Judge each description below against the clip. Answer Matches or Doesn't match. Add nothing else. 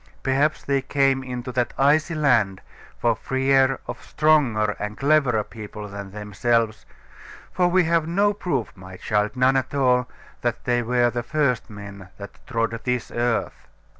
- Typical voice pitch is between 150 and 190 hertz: Doesn't match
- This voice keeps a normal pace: Matches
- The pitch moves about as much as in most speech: Matches